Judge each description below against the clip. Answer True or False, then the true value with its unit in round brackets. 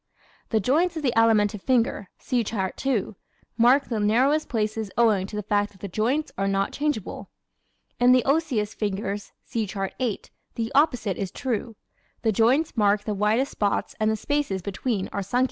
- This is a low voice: False (220 Hz)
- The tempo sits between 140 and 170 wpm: False (180 wpm)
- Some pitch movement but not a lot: True (3.8 semitones)